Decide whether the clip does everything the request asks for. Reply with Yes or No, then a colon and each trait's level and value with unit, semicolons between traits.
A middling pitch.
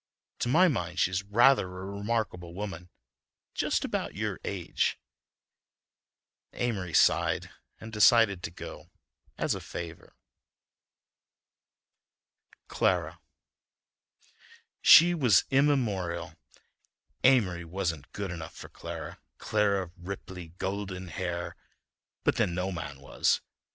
No: very low, 95 Hz